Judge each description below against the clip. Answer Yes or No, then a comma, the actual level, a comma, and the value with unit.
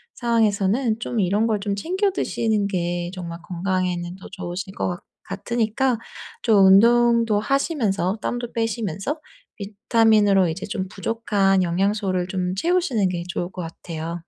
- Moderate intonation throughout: Yes, average, 3.7 semitones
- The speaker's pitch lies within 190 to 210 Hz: Yes, high, 200 Hz